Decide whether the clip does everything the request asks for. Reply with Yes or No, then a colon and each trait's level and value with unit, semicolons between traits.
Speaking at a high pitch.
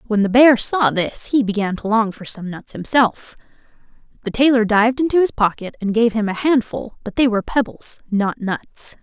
Yes: high, 225 Hz